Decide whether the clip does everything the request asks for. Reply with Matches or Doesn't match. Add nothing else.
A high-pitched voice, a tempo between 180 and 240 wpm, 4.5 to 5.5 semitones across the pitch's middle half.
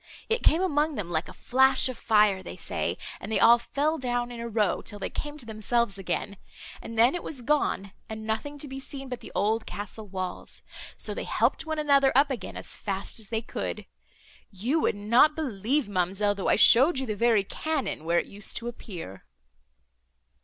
Matches